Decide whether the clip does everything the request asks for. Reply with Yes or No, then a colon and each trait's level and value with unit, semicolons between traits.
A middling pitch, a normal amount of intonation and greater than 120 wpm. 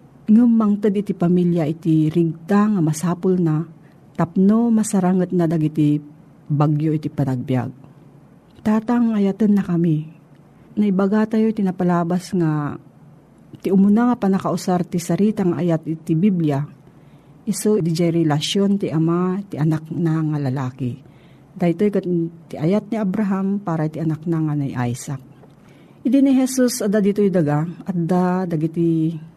Yes: medium, 170 Hz; average, 4.4 semitones; average, 145 wpm